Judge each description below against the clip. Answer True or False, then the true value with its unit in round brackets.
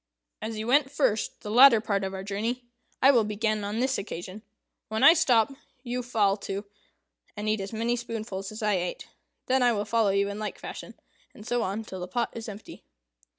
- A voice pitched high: True (220 Hz)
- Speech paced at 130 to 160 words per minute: False (205 wpm)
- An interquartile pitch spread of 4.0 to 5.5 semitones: False (3.0 semitones)